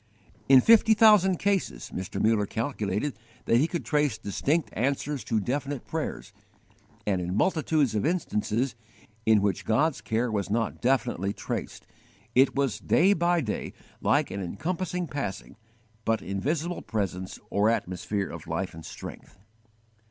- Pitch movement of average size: No, wide, 7.3 semitones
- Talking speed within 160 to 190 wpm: No, average, 140 wpm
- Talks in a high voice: No, low, 125 Hz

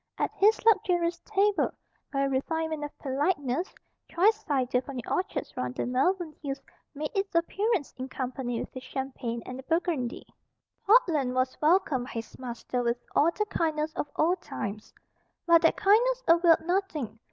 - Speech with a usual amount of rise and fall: No, wide, 5.9 semitones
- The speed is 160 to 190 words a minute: Yes, average, 165 wpm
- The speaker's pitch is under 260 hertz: No, very high, 305 Hz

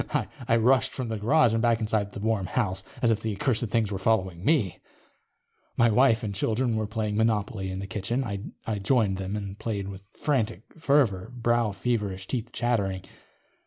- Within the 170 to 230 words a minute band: Yes, average, 185 wpm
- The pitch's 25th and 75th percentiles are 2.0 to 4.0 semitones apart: Yes, average, 3.2 semitones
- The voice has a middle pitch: No, low, 110 Hz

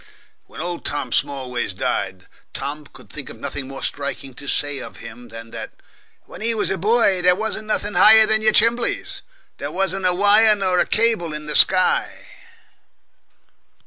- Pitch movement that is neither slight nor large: No, wide, 7.5 semitones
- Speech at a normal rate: Yes, average, 170 wpm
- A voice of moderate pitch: Yes, medium, 180 Hz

